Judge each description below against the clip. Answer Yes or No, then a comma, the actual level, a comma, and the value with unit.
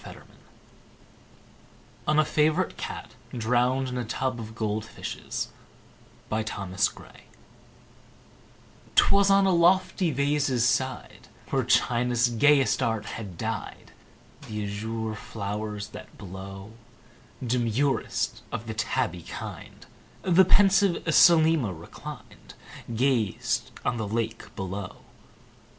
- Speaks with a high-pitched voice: No, low, 120 Hz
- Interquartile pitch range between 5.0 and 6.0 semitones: Yes, average, 5.3 semitones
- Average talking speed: No, slow, 100 wpm